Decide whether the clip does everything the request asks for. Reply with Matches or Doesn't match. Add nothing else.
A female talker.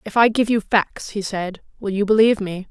Matches